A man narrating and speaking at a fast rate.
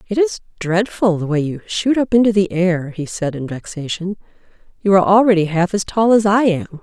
No: female; fast, 210 wpm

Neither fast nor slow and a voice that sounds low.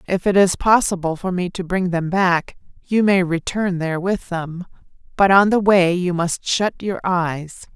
No: average, 195 wpm; medium, 180 Hz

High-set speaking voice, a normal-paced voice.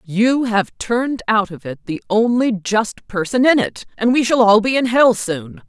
No: high, 225 Hz; fast, 210 wpm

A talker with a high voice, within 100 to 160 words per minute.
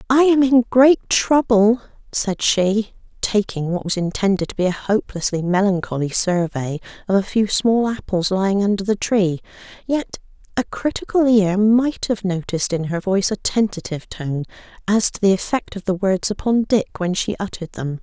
No: high, 205 Hz; average, 175 wpm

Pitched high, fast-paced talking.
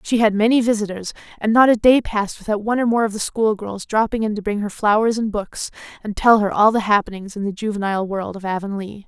Yes: high, 210 Hz; fast, 240 wpm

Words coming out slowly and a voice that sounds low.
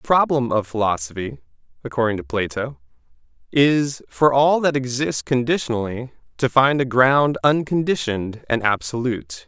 Yes: slow, 125 wpm; low, 125 Hz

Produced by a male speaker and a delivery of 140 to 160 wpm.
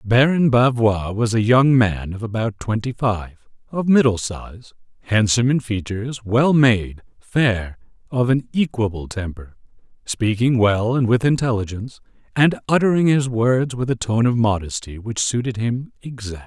Yes: male; average, 150 wpm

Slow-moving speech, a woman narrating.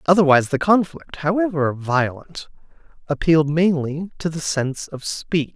No: slow, 130 wpm; male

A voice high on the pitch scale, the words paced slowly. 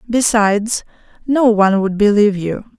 Yes: high, 215 Hz; slow, 130 wpm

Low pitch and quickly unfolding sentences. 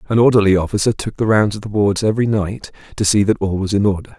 Yes: low, 105 Hz; fast, 260 wpm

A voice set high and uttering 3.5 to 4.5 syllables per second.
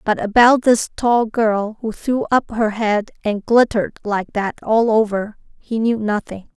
Yes: high, 220 Hz; 4.1 syllables/s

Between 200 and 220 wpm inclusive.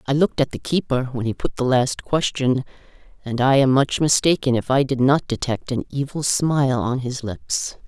Yes: fast, 205 wpm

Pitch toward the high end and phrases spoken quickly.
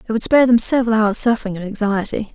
Yes: high, 220 Hz; fast, 230 wpm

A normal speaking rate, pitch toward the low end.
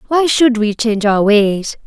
No: average, 195 wpm; high, 230 Hz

